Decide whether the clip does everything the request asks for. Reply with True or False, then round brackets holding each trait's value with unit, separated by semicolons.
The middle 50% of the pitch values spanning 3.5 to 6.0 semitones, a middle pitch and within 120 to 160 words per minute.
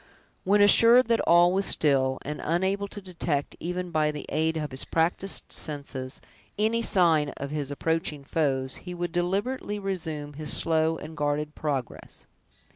True (4.3 semitones; 160 Hz; 155 wpm)